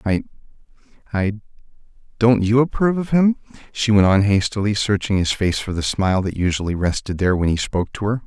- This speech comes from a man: Yes, male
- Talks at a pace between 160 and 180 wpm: Yes, average, 175 wpm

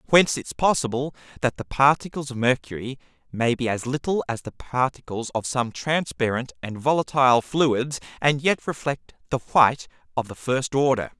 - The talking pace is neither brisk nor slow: Yes, average, 160 wpm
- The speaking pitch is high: No, low, 130 Hz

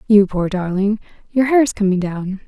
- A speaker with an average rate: Yes, average, 170 wpm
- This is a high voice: Yes, high, 205 Hz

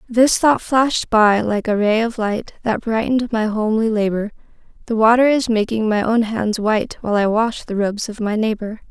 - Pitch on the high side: Yes, high, 220 Hz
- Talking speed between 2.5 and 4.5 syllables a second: No, 5.3 syllables/s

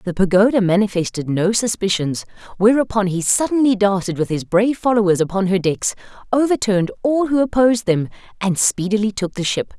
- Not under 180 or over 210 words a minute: No, average, 160 wpm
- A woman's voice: Yes, female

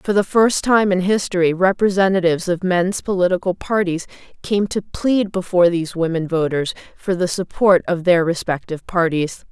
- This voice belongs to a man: No, female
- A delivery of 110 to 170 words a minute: Yes, average, 160 wpm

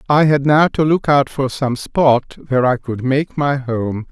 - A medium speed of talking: No, fast, 220 wpm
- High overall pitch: No, low, 135 Hz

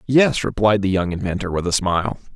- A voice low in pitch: Yes, low, 100 Hz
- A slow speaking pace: No, fast, 205 wpm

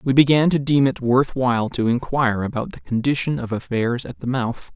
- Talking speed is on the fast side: Yes, fast, 215 wpm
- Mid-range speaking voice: No, low, 130 Hz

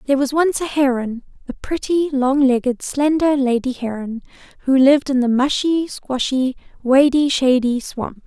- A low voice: No, very high, 270 Hz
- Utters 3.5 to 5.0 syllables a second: Yes, 4.7 syllables/s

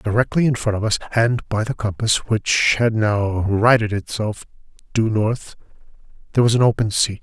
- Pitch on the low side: Yes, low, 110 Hz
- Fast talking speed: No, average, 175 wpm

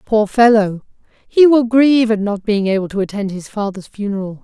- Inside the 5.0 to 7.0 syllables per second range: Yes, 5.2 syllables/s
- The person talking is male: No, female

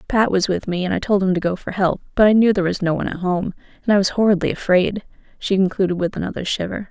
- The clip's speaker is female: Yes, female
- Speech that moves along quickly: Yes, fast, 260 wpm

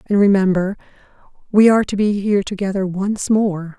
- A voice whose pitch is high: Yes, high, 200 Hz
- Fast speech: No, average, 160 wpm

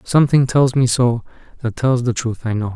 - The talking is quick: Yes, fast, 220 wpm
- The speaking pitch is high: No, low, 120 Hz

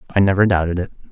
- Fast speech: Yes, fast, 215 wpm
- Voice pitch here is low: Yes, very low, 95 Hz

